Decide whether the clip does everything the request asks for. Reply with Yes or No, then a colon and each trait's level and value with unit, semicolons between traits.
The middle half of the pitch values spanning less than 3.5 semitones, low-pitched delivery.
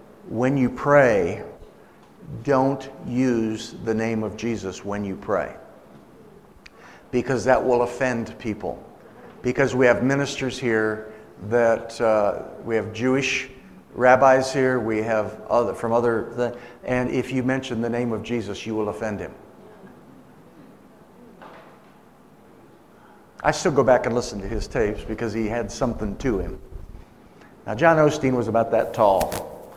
Yes: average, 2.8 semitones; low, 120 Hz